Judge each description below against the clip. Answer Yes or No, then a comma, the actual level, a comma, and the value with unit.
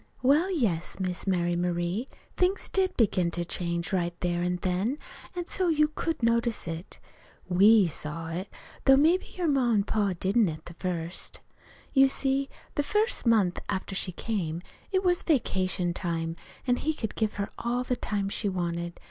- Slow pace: No, average, 175 wpm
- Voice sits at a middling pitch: No, high, 200 Hz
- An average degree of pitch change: No, wide, 7.4 semitones